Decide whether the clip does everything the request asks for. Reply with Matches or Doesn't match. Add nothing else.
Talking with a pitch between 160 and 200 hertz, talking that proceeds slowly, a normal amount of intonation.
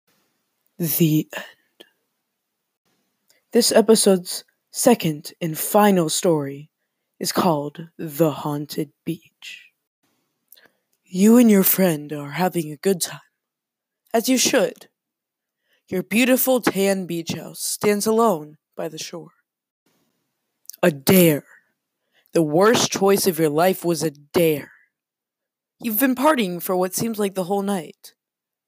Matches